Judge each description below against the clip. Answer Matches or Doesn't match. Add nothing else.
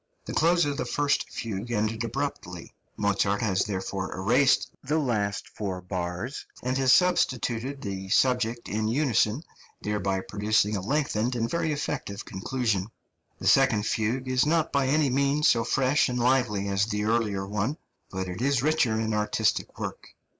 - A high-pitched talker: Doesn't match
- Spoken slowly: Doesn't match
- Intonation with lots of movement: Doesn't match